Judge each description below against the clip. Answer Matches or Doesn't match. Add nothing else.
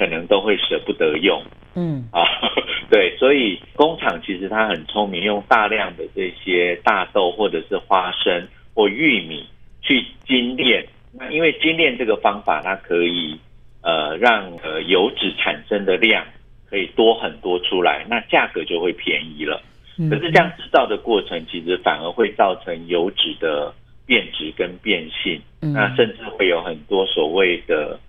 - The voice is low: Matches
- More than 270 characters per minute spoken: Doesn't match